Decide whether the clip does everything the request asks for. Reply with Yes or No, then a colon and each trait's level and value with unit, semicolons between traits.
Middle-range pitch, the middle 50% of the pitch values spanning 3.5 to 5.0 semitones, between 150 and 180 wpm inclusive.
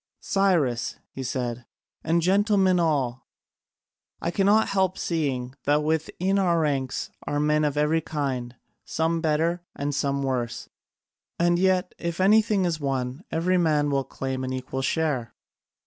No: medium, 155 Hz; average, 4.7 semitones; average, 140 wpm